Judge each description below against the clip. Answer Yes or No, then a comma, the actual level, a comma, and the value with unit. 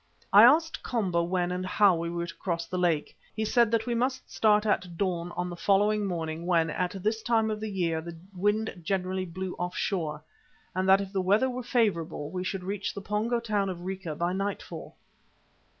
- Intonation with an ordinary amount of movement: Yes, average, 3.4 semitones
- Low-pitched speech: No, high, 190 Hz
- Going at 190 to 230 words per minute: Yes, fast, 205 wpm